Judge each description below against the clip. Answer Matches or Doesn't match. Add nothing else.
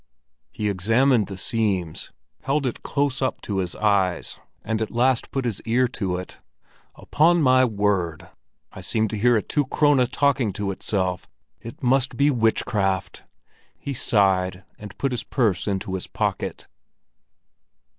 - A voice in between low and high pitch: Doesn't match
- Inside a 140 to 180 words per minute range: Matches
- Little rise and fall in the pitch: Doesn't match